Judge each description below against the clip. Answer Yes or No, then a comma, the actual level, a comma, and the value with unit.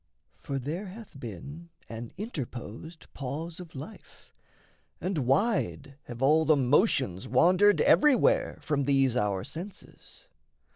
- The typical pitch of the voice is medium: Yes, medium, 145 Hz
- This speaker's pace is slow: Yes, slow, 115 wpm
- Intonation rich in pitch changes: Yes, wide, 5.8 semitones